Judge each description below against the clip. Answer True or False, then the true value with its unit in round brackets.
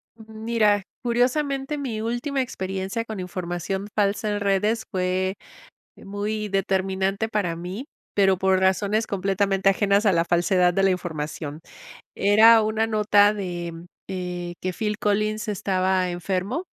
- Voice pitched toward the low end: False (195 Hz)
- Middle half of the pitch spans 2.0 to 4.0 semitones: True (2.6 semitones)